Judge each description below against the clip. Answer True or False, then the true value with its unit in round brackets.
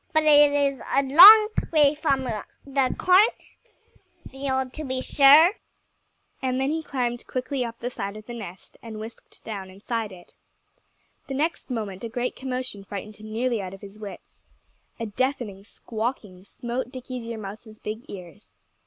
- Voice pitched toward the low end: False (245 Hz)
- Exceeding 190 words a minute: False (160 wpm)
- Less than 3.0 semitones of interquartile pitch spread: False (4.2 semitones)